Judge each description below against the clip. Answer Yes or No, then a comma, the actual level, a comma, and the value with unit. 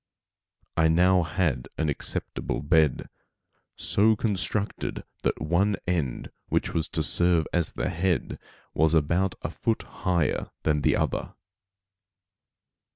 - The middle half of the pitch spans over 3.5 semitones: No, average, 3.1 semitones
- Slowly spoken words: Yes, slow, 120 wpm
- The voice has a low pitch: Yes, very low, 85 Hz